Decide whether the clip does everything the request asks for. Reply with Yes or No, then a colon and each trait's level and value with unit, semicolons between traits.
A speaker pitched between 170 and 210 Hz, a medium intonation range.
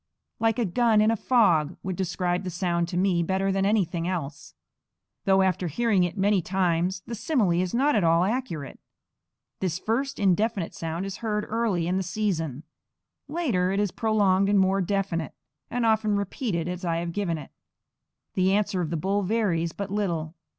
Yes: high, 190 Hz; average, 3.6 semitones